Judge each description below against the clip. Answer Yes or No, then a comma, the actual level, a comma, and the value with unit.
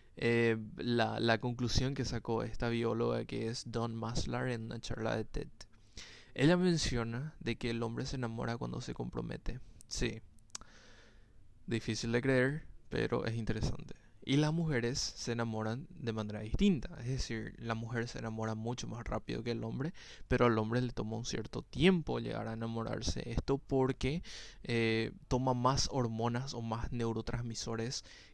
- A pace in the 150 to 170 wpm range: Yes, average, 160 wpm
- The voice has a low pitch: Yes, low, 115 Hz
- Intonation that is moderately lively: No, narrow, 1.9 semitones